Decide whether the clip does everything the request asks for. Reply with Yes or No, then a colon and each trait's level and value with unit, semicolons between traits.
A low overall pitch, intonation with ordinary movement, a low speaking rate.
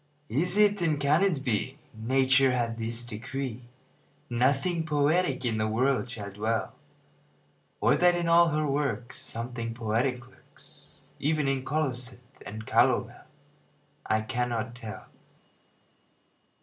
Yes: low, 130 Hz; average, 4.1 semitones; slow, 125 wpm